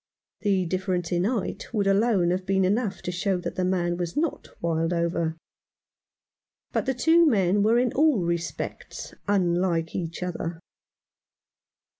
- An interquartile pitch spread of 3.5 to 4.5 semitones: No, average, 3.1 semitones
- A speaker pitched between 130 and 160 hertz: No, medium, 185 Hz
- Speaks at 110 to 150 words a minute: Yes, average, 140 wpm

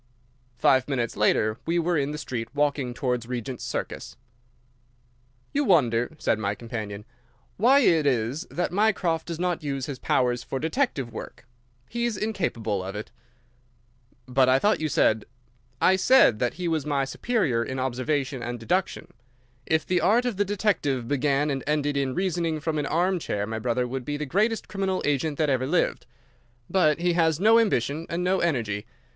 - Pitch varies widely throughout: Yes, wide, 6.2 semitones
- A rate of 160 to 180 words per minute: Yes, average, 175 wpm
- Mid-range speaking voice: Yes, medium, 145 Hz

